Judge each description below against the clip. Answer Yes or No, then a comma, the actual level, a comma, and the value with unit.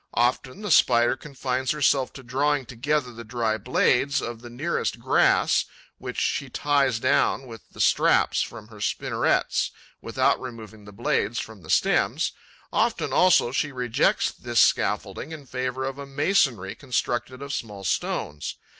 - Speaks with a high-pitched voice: No, low, 125 Hz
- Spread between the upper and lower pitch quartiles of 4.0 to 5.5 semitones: No, average, 3.3 semitones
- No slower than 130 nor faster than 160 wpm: Yes, average, 150 wpm